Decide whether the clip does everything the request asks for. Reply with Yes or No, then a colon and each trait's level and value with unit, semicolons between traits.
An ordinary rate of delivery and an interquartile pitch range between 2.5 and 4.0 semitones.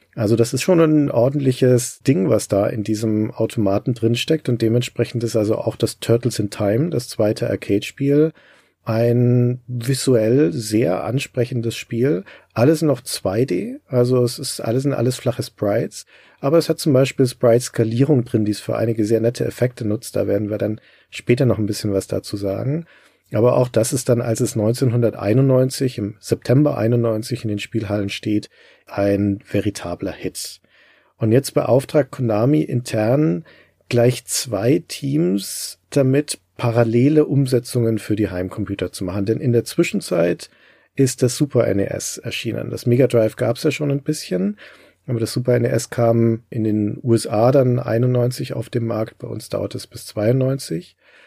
Yes: average, 165 wpm; average, 3.4 semitones